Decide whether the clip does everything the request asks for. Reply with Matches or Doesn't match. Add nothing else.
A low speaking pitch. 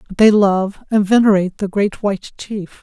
Doesn't match